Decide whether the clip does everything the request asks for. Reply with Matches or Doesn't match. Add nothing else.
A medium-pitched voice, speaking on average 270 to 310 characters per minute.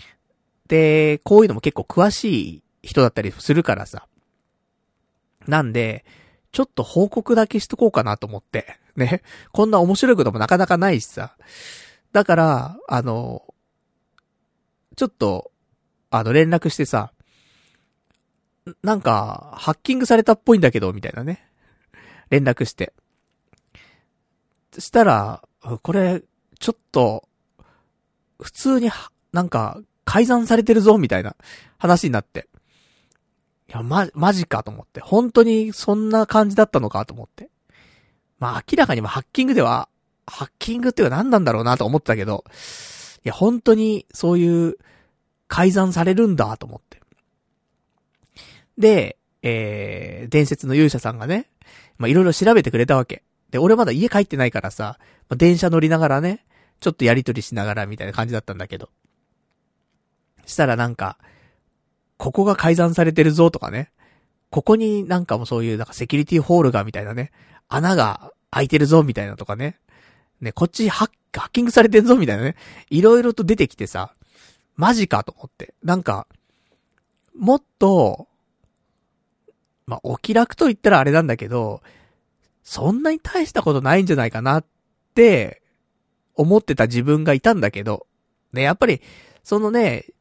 Matches